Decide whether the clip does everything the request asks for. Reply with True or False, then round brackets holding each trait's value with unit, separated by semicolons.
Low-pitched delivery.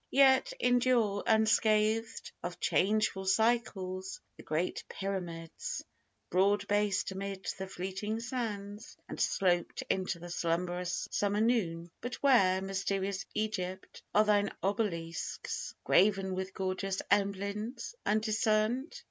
False (200 Hz)